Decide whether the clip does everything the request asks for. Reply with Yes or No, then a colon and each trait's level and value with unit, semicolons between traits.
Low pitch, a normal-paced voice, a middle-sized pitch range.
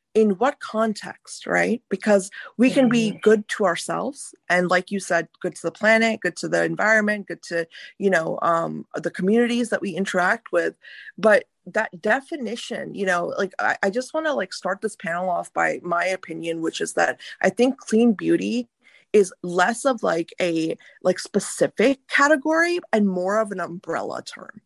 No: high, 200 Hz; average, 180 wpm; average, 4.8 semitones